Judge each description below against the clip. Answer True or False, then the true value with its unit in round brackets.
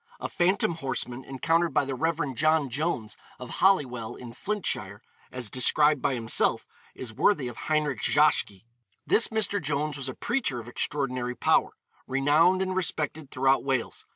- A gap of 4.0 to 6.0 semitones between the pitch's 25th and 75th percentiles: True (4.7 semitones)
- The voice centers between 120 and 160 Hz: True (140 Hz)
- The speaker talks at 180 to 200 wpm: False (155 wpm)